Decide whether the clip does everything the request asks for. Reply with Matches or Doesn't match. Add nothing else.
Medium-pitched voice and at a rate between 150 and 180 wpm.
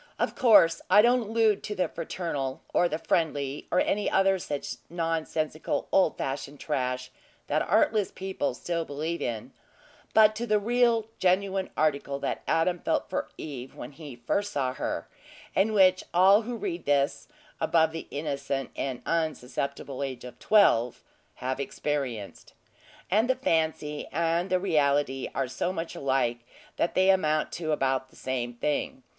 Matches